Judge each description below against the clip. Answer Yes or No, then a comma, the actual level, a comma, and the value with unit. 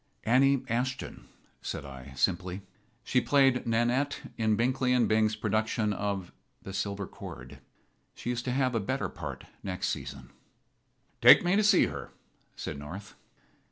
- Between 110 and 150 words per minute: Yes, average, 145 wpm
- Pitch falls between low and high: No, low, 110 Hz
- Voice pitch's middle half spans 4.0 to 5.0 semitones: Yes, average, 4.6 semitones